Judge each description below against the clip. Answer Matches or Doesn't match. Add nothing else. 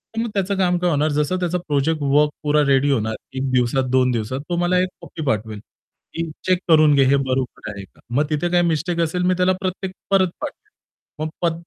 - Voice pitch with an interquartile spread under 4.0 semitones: Doesn't match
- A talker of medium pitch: Matches